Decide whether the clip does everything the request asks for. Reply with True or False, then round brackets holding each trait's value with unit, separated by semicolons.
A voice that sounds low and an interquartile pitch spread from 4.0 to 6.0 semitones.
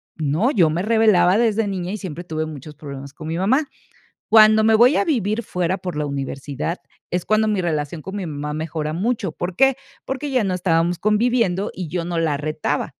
False (180 Hz; 5.5 semitones)